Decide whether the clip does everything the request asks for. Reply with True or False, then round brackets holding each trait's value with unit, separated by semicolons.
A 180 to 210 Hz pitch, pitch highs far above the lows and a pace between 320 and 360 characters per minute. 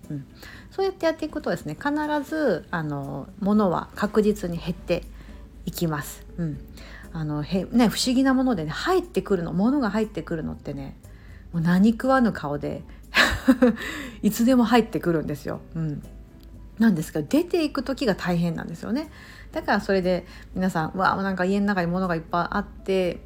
True (190 Hz; 6.7 semitones; 345 characters per minute)